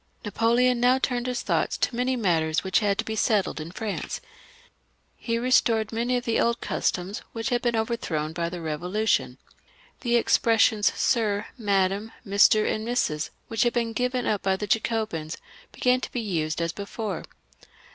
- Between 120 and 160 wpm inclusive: No, average, 170 wpm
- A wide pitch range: No, average, 3.9 semitones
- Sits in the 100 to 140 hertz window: No, high, 220 Hz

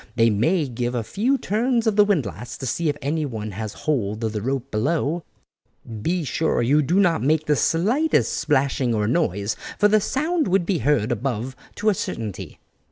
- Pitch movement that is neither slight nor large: No, wide, 7.9 semitones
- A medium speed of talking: Yes, average, 185 wpm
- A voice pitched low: No, medium, 145 Hz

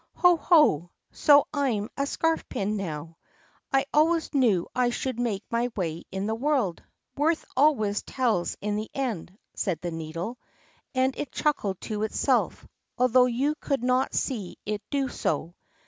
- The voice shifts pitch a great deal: Yes, wide, 6.0 semitones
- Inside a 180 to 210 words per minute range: No, average, 155 wpm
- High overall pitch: Yes, high, 240 Hz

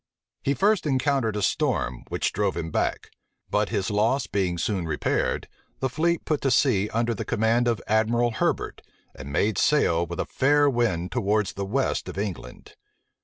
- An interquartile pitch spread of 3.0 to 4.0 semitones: No, average, 5.2 semitones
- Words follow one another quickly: No, average, 170 wpm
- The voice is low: Yes, low, 110 Hz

